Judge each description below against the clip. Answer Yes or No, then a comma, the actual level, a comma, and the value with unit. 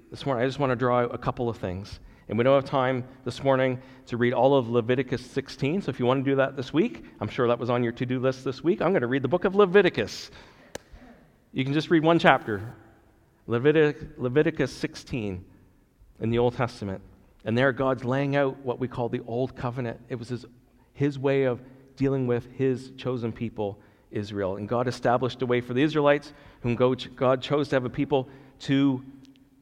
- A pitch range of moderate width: No, narrow, 2.3 semitones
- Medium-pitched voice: No, low, 130 Hz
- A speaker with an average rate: No, fast, 210 wpm